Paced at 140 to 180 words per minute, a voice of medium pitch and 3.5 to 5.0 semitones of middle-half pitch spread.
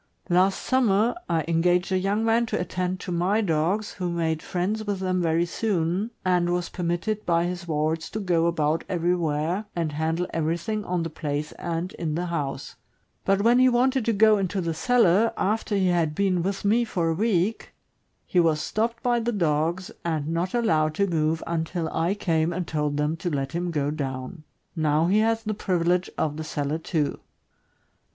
No: average, 190 wpm; medium, 175 Hz; average, 3.8 semitones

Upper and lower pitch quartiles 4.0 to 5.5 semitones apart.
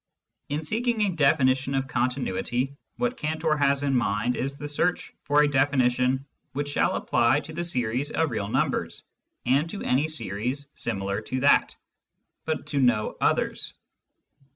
No: average, 3.3 semitones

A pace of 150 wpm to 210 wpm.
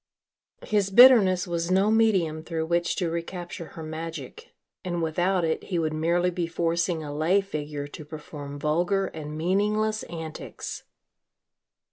No: average, 140 wpm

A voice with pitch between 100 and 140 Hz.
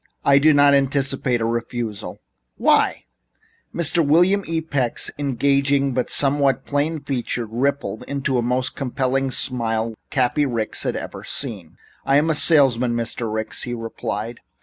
Yes: low, 135 Hz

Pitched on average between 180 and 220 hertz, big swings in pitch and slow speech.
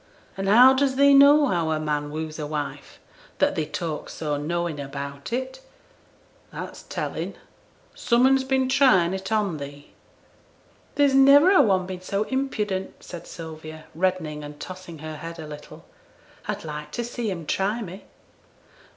No: medium, 185 Hz; wide, 8.0 semitones; average, 160 wpm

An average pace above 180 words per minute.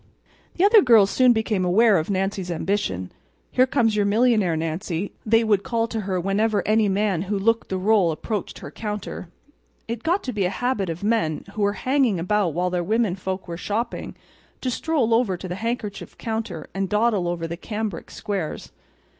Yes: average, 190 wpm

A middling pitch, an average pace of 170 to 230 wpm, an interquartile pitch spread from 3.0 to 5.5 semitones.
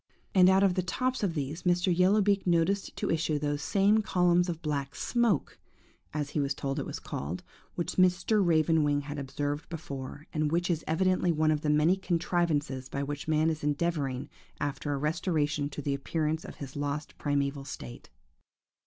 Yes: medium, 155 Hz; average, 185 wpm; average, 3.6 semitones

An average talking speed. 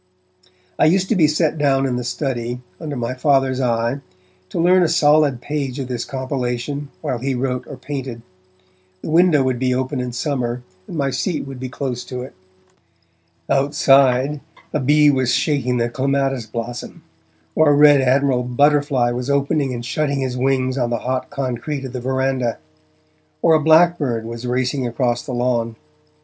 Yes: average, 170 wpm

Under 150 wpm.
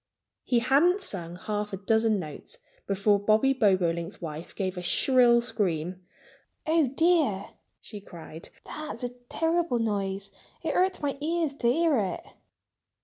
Yes: average, 140 wpm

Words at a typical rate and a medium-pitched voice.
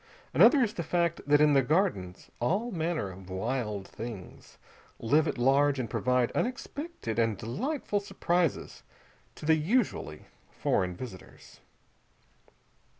No: slow, 125 wpm; medium, 145 Hz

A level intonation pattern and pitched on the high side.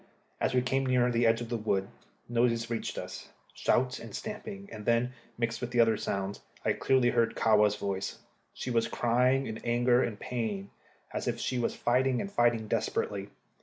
No: narrow, 2.0 semitones; low, 120 Hz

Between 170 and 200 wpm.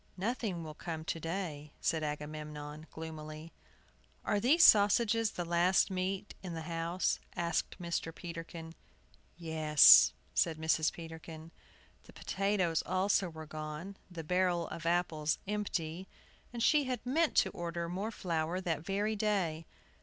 No: slow, 135 wpm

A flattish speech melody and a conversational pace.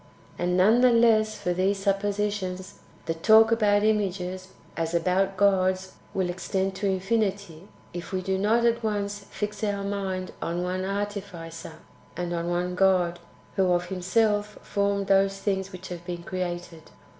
Yes: narrow, 2.3 semitones; average, 155 wpm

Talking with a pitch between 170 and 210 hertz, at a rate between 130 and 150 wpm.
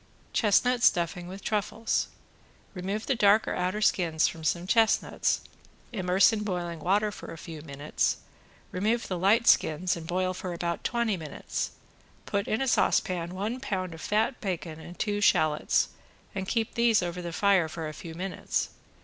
No: medium, 185 Hz; average, 165 wpm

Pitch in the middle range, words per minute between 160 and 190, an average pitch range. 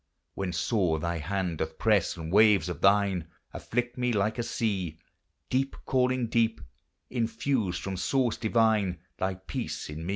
No: low, 100 Hz; average, 165 wpm; average, 4.5 semitones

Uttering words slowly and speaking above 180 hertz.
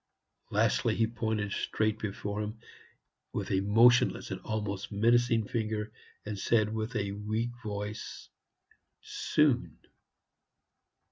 No: slow, 110 wpm; low, 110 Hz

